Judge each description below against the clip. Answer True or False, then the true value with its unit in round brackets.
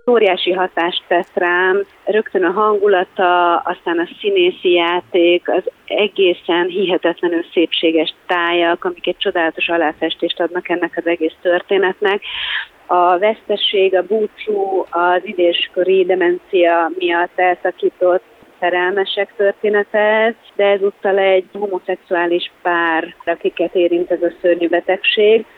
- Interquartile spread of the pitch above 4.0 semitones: False (2.7 semitones)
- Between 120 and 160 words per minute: False (110 wpm)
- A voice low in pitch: False (180 Hz)